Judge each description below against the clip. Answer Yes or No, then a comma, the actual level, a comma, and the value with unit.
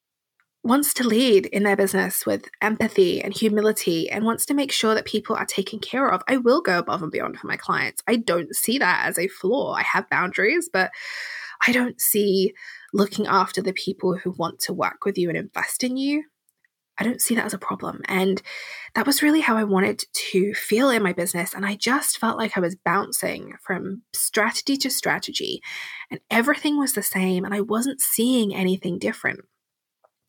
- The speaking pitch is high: Yes, high, 215 Hz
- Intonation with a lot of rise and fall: No, average, 4.8 semitones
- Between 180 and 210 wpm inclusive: Yes, average, 200 wpm